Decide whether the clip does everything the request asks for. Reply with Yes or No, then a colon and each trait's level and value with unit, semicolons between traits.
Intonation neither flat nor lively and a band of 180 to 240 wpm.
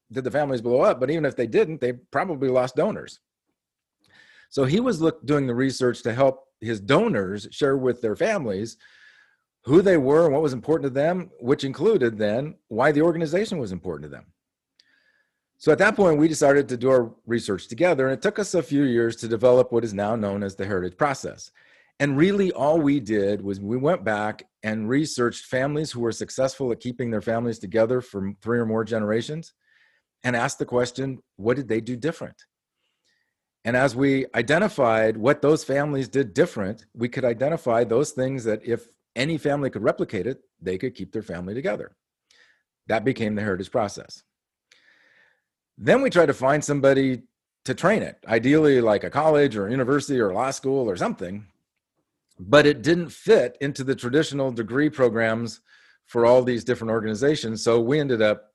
Yes: average, 4.2 semitones; average, 185 wpm